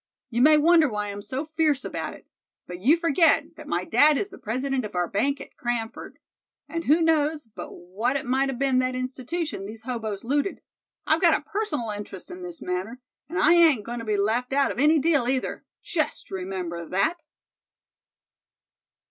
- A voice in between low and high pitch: No, very high, 260 Hz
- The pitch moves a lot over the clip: Yes, wide, 6.1 semitones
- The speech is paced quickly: No, average, 190 wpm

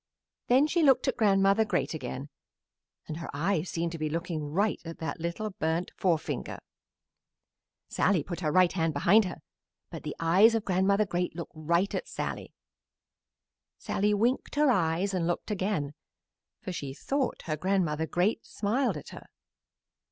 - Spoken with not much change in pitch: No, average, 4.1 semitones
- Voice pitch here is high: No, medium, 180 Hz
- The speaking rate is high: No, average, 160 wpm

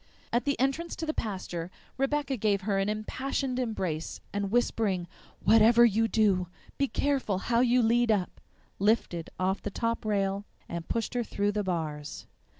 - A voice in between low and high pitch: No, high, 215 Hz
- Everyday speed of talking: Yes, average, 160 wpm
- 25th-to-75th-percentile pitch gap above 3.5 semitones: Yes, average, 3.9 semitones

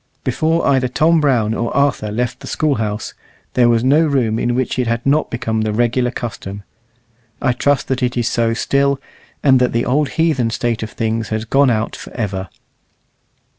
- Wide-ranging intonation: No, average, 3.3 semitones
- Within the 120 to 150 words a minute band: No, average, 185 wpm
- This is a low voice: Yes, low, 120 Hz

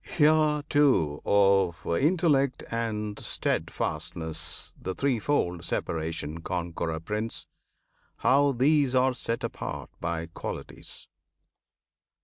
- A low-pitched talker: Yes, low, 105 Hz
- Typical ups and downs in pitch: No, wide, 8.7 semitones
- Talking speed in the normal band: No, slow, 90 wpm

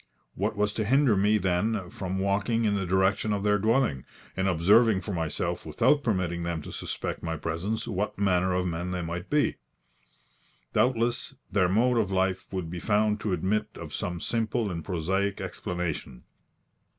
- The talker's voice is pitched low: Yes, very low, 95 Hz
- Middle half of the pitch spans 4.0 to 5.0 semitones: No, average, 3.3 semitones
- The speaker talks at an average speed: Yes, average, 170 wpm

